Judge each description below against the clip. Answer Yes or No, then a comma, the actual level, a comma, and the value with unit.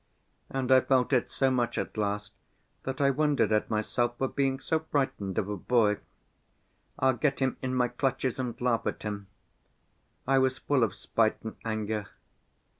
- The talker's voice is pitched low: Yes, low, 125 Hz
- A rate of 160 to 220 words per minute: Yes, average, 175 wpm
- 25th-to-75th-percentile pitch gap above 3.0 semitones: Yes, average, 3.6 semitones